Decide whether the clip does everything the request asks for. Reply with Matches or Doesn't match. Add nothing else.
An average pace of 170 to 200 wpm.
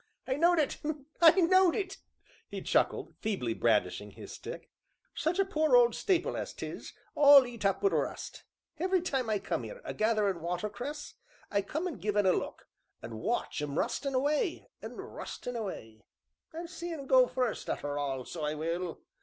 Matches